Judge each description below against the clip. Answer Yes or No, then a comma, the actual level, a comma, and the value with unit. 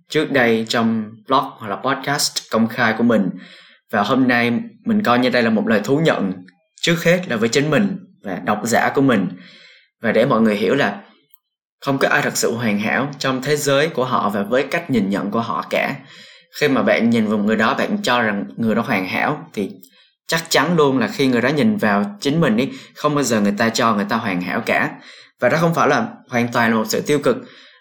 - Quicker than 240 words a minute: No, average, 235 wpm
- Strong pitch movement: Yes, wide, 6.5 semitones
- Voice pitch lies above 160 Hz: No, low, 135 Hz